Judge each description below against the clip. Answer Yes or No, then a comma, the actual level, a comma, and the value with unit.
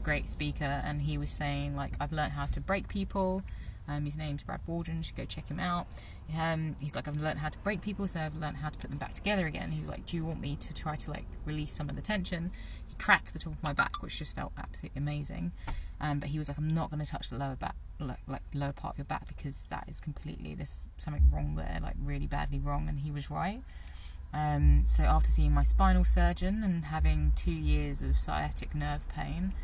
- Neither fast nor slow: No, fast, 240 wpm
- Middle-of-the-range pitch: Yes, medium, 145 Hz